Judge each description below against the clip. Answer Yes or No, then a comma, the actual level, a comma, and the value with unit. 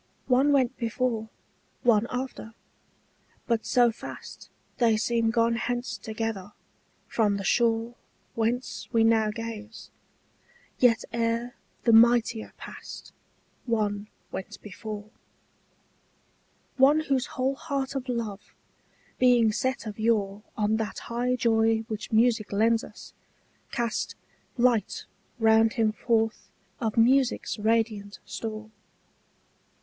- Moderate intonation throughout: No, narrow, 1.9 semitones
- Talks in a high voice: Yes, high, 230 Hz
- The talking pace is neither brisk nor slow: No, slow, 110 wpm